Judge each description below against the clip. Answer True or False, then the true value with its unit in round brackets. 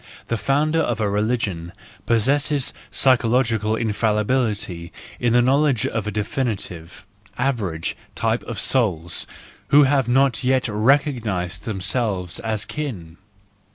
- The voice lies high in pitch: False (115 Hz)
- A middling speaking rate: False (115 wpm)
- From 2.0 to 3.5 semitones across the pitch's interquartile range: False (4.2 semitones)